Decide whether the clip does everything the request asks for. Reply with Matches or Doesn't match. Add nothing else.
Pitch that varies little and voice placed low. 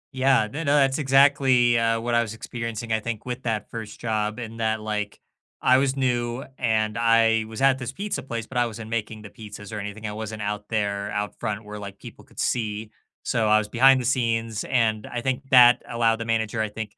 Matches